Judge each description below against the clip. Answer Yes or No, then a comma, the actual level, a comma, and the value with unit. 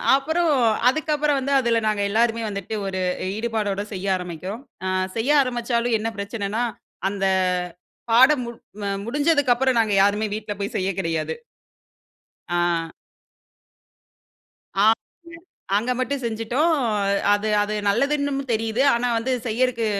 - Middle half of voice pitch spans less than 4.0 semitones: No, average, 4.3 semitones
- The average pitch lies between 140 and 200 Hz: No, high, 230 Hz